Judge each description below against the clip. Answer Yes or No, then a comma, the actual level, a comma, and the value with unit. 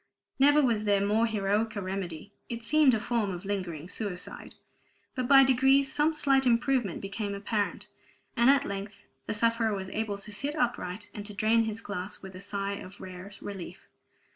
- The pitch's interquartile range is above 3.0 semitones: Yes, average, 3.5 semitones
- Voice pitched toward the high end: Yes, high, 210 Hz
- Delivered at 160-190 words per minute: Yes, average, 170 wpm